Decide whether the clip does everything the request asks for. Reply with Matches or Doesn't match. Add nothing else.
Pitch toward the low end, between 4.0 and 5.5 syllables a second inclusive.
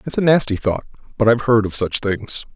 Doesn't match